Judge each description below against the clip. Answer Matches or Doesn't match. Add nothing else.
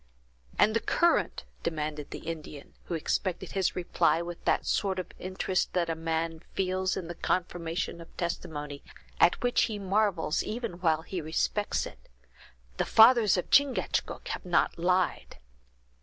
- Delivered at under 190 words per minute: Matches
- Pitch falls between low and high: Matches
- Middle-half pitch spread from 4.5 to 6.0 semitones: Doesn't match